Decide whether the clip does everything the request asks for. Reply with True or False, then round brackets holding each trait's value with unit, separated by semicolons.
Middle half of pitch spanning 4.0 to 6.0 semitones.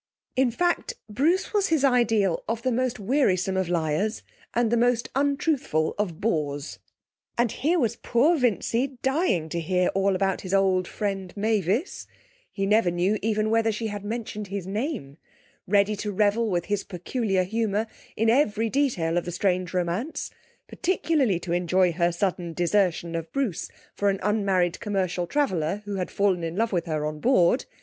True (4.8 semitones)